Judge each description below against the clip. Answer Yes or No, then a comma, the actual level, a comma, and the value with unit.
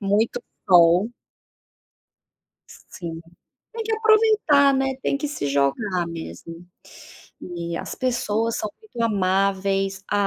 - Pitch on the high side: Yes, high, 200 Hz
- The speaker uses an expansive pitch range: Yes, wide, 7.3 semitones